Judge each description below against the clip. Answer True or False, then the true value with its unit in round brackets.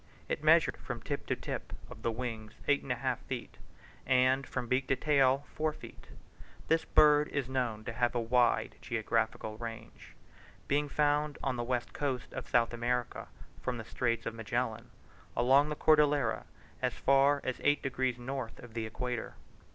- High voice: False (125 Hz)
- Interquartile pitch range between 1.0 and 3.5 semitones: True (2.8 semitones)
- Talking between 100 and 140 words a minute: False (175 wpm)